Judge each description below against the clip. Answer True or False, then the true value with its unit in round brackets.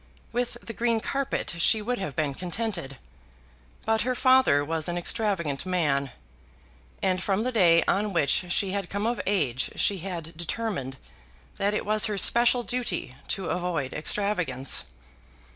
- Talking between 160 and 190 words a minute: False (150 wpm)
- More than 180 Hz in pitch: True (190 Hz)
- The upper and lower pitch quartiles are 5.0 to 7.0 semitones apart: True (5.4 semitones)